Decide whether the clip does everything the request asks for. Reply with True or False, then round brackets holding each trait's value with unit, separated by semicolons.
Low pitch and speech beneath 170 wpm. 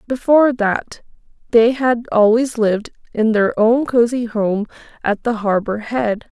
False (230 Hz; 140 wpm)